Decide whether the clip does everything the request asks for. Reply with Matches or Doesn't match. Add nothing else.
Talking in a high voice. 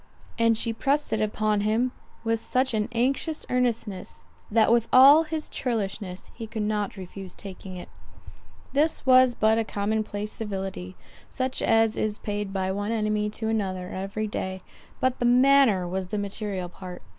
Matches